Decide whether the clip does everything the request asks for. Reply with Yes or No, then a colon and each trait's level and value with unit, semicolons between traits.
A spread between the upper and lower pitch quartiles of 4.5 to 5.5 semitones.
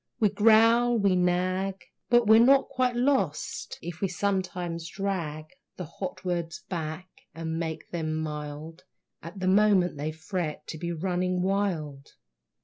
No: average, 3.8 semitones